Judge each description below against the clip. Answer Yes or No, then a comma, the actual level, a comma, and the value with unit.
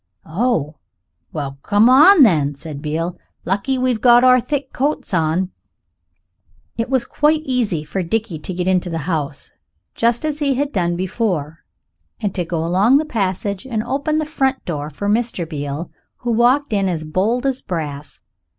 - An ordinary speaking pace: Yes, average, 170 wpm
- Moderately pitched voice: No, high, 200 Hz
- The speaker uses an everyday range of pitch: No, wide, 7.5 semitones